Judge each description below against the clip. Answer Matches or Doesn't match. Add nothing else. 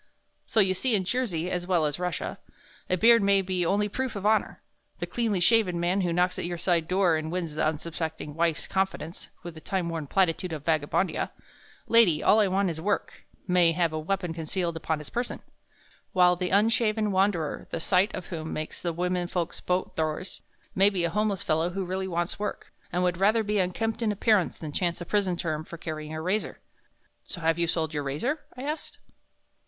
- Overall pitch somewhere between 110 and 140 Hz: Doesn't match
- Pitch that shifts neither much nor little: Matches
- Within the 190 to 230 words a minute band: Matches